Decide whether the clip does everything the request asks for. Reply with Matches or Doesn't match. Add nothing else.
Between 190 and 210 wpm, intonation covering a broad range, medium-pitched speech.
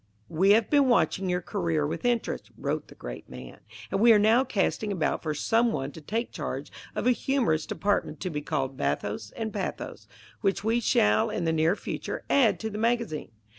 Doesn't match